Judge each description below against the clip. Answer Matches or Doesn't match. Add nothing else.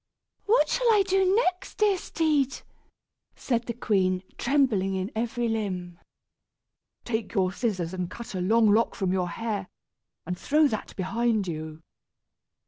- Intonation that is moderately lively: Doesn't match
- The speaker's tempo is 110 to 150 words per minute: Matches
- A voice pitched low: Doesn't match